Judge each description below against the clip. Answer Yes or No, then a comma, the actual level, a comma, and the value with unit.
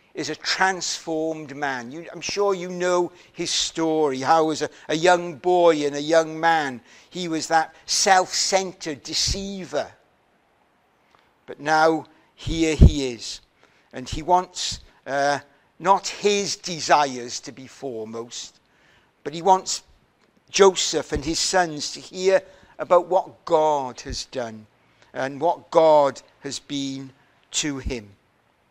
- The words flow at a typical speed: No, slow, 130 wpm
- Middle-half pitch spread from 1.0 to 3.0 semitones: No, average, 4.3 semitones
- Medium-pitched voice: Yes, medium, 160 Hz